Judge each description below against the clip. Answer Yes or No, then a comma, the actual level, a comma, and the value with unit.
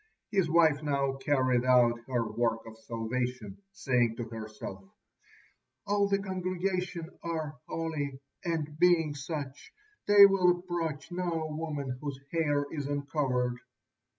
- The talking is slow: Yes, slow, 125 wpm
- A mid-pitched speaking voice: Yes, medium, 145 Hz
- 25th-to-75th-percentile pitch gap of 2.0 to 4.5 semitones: No, average, 5.2 semitones